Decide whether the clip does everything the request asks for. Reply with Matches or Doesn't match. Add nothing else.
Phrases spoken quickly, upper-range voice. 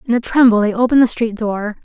Matches